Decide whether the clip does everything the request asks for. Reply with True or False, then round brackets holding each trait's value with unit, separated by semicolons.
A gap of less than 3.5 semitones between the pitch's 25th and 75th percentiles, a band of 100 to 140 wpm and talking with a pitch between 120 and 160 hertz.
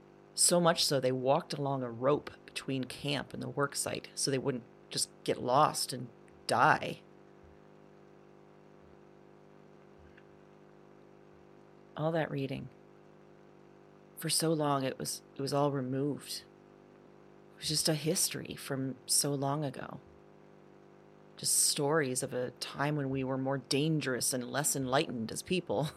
True (2.9 semitones; 135 wpm; 140 Hz)